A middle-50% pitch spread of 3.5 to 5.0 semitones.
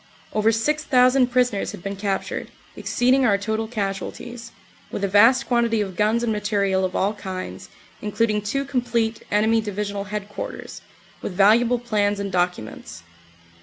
No: average, 3.0 semitones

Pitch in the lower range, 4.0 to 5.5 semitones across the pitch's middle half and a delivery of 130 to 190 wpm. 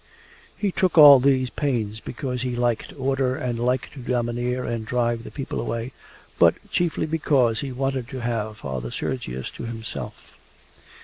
No: low, 125 Hz; narrow, 2.4 semitones; average, 160 wpm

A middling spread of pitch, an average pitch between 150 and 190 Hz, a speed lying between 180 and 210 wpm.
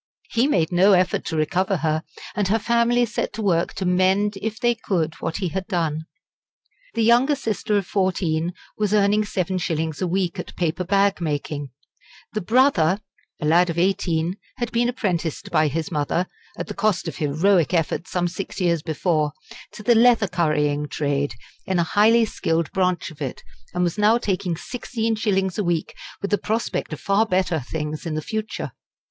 Yes: average, 4.5 semitones; medium, 185 Hz; average, 185 wpm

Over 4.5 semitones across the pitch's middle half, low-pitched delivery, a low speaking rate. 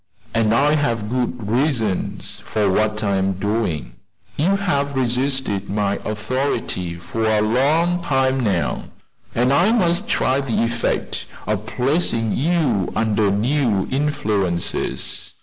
Yes: average, 5.1 semitones; low, 115 Hz; slow, 125 wpm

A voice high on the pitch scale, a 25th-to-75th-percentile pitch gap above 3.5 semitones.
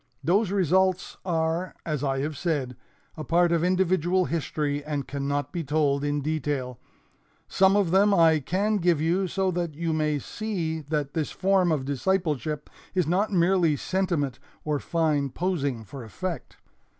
No: medium, 160 Hz; average, 4.1 semitones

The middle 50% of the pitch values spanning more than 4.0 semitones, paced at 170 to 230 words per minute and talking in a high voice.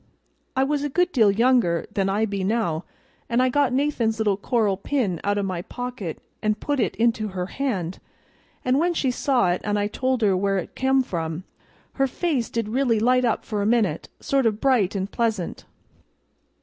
Yes: average, 4.7 semitones; average, 200 wpm; high, 225 Hz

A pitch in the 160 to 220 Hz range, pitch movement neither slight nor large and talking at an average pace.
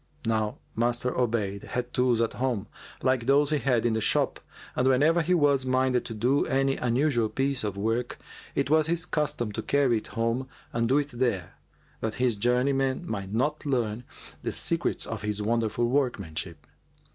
No: low, 125 Hz; average, 3.3 semitones; average, 175 wpm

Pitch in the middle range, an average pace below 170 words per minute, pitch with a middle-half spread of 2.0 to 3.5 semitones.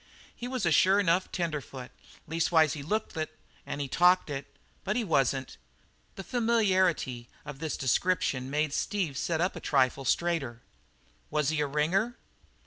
No: medium, 160 Hz; average, 155 wpm; average, 5.0 semitones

